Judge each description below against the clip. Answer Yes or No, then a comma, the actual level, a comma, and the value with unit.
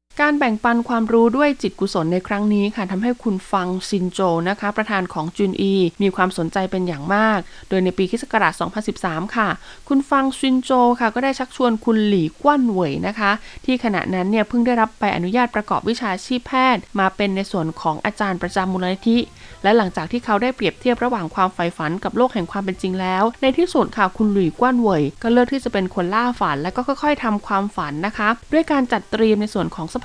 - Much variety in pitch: No, average, 4.4 semitones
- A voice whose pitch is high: Yes, high, 210 Hz